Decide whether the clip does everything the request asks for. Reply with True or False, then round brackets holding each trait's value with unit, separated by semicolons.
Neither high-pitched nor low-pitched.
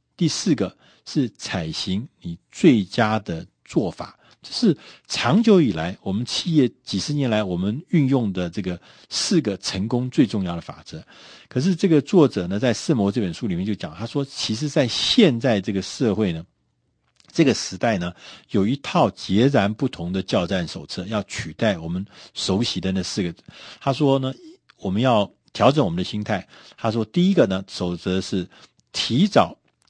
False (105 Hz)